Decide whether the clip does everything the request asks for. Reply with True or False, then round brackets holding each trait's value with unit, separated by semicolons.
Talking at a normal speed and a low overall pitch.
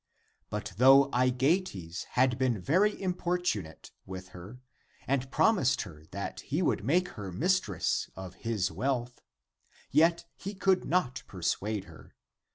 False (130 wpm; 125 Hz)